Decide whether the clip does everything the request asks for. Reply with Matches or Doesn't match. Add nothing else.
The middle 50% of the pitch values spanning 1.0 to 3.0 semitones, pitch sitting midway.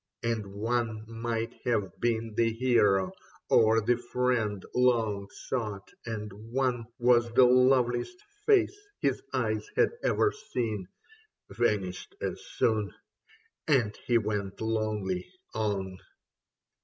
Doesn't match